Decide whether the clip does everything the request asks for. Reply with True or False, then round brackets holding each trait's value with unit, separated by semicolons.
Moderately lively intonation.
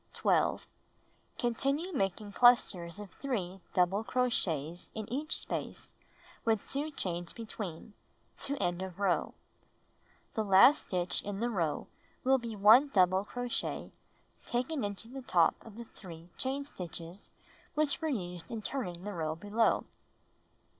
False (5.7 semitones)